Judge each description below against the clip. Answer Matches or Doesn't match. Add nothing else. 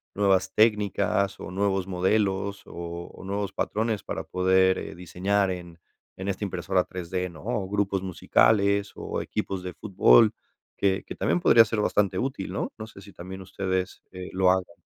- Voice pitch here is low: Matches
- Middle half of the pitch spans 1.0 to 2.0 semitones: Matches